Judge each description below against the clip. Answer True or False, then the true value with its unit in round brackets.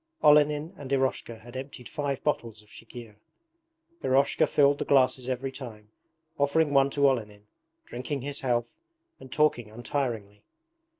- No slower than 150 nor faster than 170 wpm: False (135 wpm)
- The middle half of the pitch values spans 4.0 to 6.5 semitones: False (3.3 semitones)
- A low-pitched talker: True (130 Hz)